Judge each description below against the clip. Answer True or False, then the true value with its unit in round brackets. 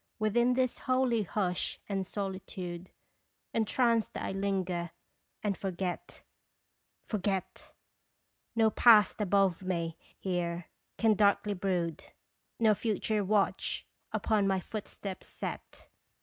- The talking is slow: True (100 wpm)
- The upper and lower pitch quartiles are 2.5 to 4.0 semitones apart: True (2.8 semitones)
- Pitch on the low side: False (195 Hz)